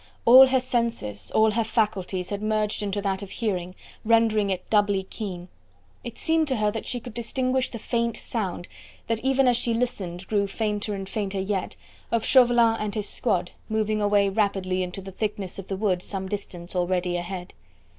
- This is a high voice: Yes, high, 210 Hz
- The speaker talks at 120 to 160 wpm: No, average, 185 wpm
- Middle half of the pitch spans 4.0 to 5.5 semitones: No, average, 3.3 semitones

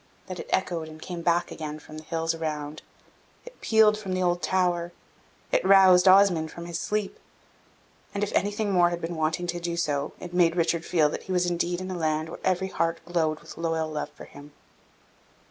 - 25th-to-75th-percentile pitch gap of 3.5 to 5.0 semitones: No, narrow, 2.5 semitones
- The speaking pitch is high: No, medium, 175 Hz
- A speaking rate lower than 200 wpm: No, fast, 205 wpm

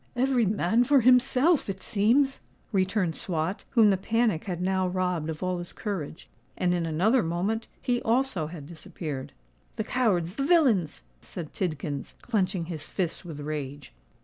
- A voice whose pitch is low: No, medium, 185 Hz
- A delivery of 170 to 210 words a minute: No, average, 150 wpm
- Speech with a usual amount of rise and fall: No, wide, 5.7 semitones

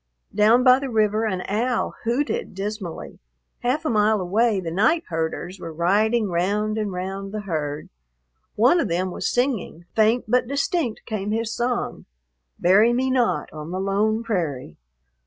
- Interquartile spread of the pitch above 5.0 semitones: No, average, 4.3 semitones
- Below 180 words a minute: Yes, average, 155 wpm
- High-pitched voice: Yes, high, 215 Hz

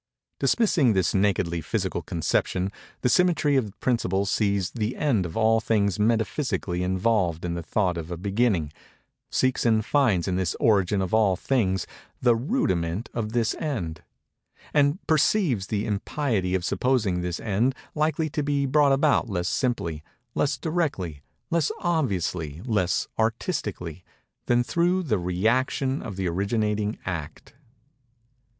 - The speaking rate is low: Yes, slow, 130 wpm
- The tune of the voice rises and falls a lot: Yes, wide, 6.3 semitones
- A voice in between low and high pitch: No, low, 110 Hz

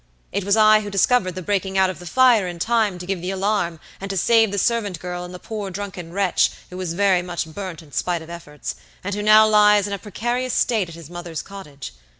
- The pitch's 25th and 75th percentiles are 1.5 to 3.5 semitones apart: Yes, average, 2.8 semitones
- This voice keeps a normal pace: No, fast, 240 wpm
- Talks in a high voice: Yes, high, 195 Hz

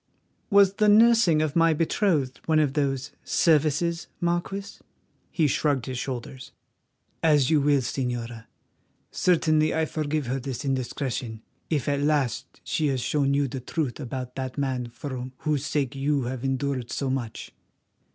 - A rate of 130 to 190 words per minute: Yes, average, 150 wpm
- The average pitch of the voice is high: No, medium, 140 Hz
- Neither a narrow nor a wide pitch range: Yes, average, 3.3 semitones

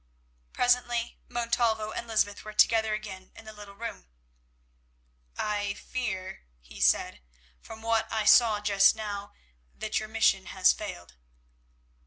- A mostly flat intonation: Yes, narrow, 2.1 semitones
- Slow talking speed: Yes, slow, 130 wpm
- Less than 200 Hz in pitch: No, high, 215 Hz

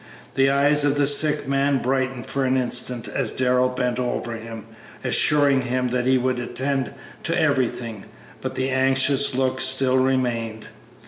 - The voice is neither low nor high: No, low, 130 Hz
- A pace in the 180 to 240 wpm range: No, average, 155 wpm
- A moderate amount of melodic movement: No, narrow, 1.7 semitones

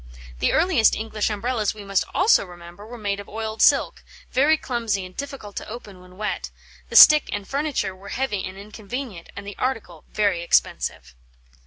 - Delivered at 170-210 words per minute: Yes, average, 175 wpm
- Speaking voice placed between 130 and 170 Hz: No, high, 210 Hz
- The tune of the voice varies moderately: Yes, average, 4.0 semitones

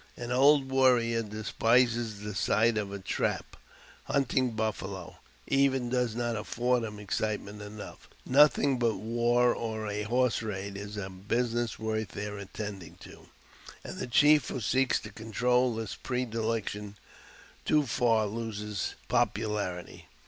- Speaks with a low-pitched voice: Yes, low, 115 Hz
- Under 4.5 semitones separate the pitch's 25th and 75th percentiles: Yes, average, 2.9 semitones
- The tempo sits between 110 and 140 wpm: Yes, slow, 135 wpm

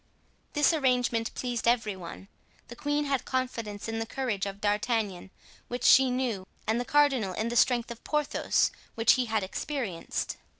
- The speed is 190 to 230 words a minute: No, average, 165 wpm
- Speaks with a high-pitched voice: Yes, high, 235 Hz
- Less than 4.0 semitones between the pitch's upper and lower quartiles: Yes, average, 3.6 semitones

